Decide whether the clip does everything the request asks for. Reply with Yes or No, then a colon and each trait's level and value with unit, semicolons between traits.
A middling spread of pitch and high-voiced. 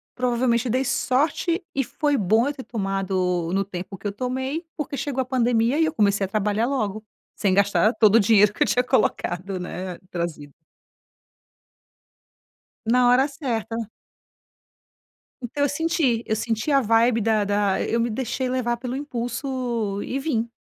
Yes: average, 4.2 semitones; high, 235 Hz